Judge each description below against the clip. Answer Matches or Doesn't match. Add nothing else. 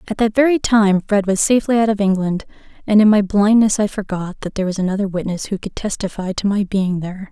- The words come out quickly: Matches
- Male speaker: Doesn't match